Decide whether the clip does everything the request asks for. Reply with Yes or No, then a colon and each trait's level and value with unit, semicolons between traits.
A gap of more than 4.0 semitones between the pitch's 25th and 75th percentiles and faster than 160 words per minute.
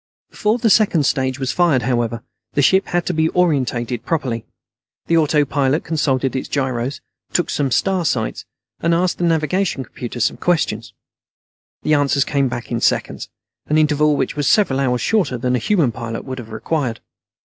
Yes: average, 4.8 semitones; average, 170 wpm